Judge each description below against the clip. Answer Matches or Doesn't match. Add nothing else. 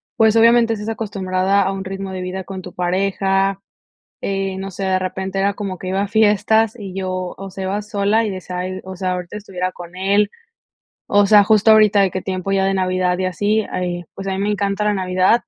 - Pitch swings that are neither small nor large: Doesn't match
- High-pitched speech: Matches